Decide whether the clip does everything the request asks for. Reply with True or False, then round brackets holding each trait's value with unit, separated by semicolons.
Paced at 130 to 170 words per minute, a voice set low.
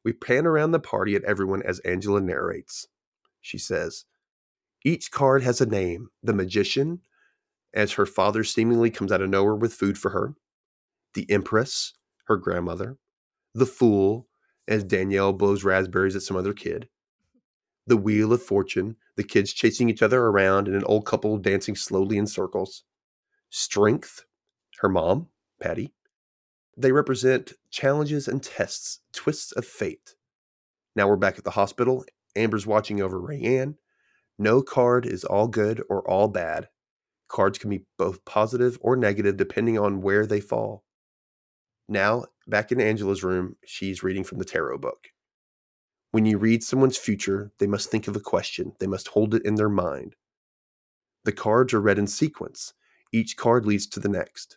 True (160 wpm; 105 Hz)